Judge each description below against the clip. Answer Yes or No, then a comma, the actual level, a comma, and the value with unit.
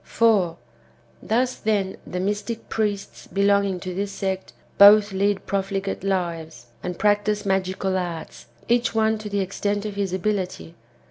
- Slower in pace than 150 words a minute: Yes, average, 140 wpm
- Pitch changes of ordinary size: No, narrow, 1.9 semitones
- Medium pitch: No, high, 200 Hz